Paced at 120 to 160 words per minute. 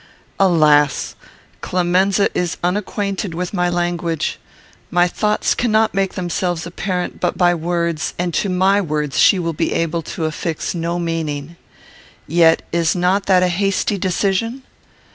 Yes: average, 140 wpm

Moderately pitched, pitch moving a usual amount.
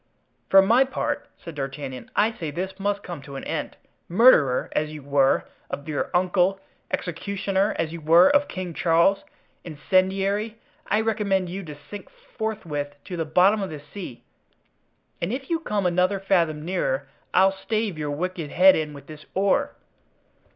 Yes: medium, 180 Hz; average, 4.5 semitones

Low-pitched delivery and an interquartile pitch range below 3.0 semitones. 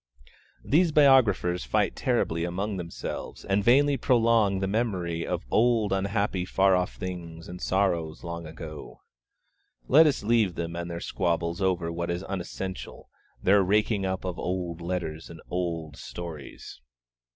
No: very low, 90 Hz; average, 3.3 semitones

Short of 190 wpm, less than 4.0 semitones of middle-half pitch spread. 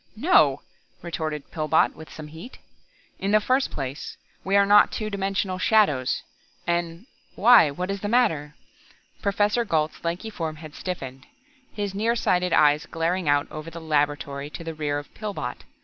No: average, 160 wpm; average, 5.1 semitones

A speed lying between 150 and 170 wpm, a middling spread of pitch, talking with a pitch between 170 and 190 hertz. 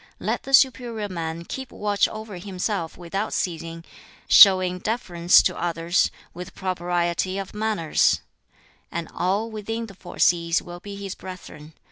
No: average, 140 wpm; average, 3.4 semitones; medium, 185 Hz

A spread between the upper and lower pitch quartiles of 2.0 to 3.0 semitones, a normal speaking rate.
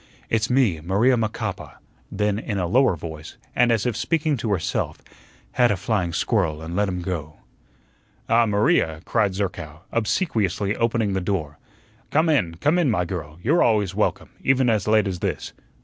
No: average, 4.9 semitones; average, 170 wpm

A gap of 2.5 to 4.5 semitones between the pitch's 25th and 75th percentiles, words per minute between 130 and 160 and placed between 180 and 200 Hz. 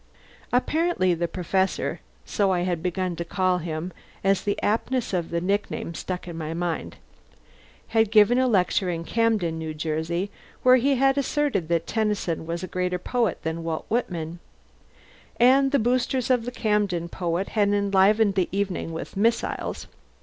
No: average, 4.9 semitones; average, 155 wpm; high, 190 Hz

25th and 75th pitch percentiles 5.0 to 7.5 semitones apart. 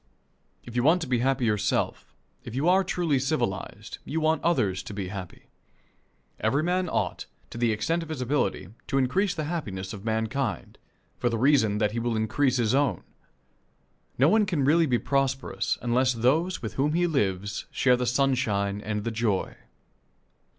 Yes: average, 5.3 semitones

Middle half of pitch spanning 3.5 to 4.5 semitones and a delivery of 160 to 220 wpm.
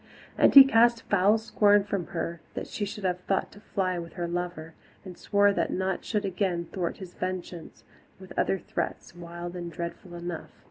No: average, 2.7 semitones; average, 185 wpm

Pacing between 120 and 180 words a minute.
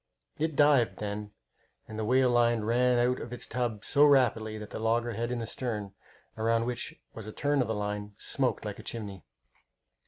No: average, 190 wpm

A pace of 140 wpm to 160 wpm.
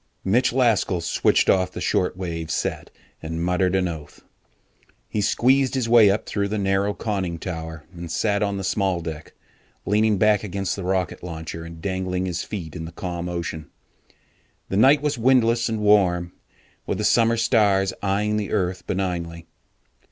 No: average, 170 wpm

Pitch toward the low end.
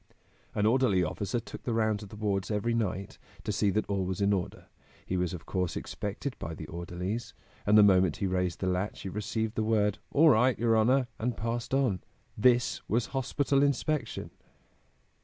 Yes: low, 105 Hz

